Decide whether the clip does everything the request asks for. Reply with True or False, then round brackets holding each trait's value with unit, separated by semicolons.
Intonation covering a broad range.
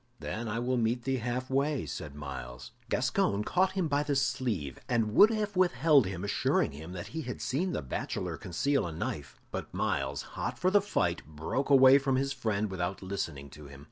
True (8.7 semitones)